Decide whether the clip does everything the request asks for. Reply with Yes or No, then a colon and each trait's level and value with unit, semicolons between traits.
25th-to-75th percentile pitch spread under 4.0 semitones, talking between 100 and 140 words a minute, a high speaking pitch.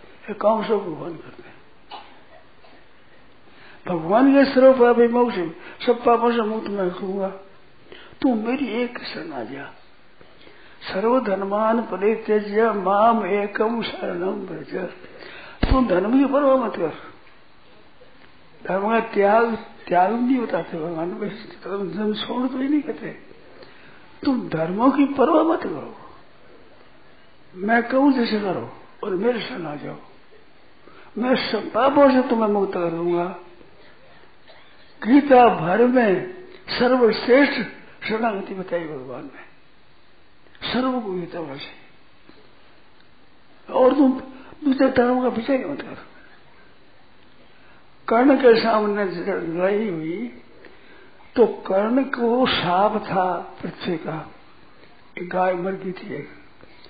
No: average, 5.1 semitones; average, 115 wpm; high, 220 Hz